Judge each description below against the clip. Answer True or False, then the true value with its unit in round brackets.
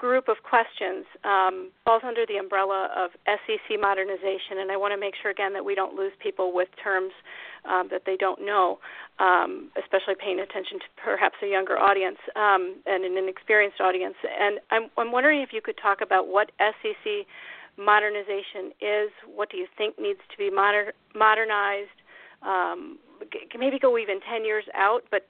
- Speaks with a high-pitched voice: True (205 Hz)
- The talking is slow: False (180 wpm)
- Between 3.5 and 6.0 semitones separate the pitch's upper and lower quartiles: False (3.0 semitones)